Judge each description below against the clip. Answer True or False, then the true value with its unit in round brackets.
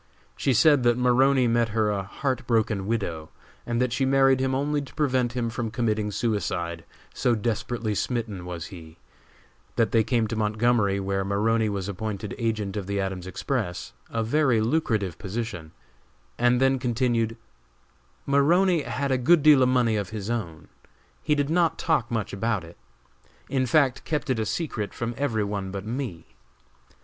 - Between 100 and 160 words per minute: False (170 wpm)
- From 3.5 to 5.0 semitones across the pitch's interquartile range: True (4.2 semitones)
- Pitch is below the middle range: True (115 Hz)